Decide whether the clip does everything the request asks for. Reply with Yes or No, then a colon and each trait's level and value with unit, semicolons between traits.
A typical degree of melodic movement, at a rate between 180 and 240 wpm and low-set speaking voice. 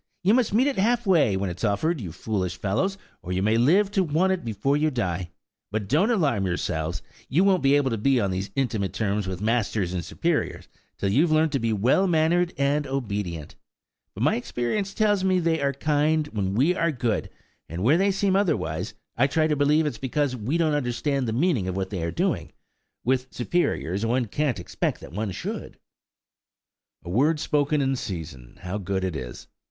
No: wide, 8.1 semitones; average, 200 wpm; low, 130 Hz